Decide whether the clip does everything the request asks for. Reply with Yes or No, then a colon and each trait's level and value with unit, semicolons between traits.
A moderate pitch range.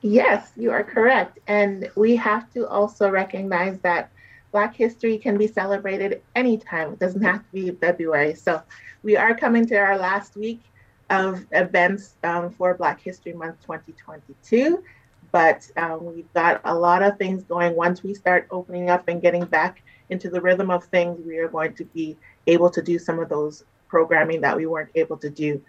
Yes: average, 3.3 semitones